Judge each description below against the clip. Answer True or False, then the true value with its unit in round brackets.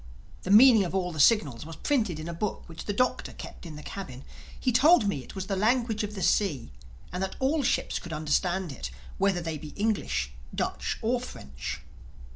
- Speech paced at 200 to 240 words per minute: True (205 wpm)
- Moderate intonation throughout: False (5.7 semitones)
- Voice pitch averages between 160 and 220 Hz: True (190 Hz)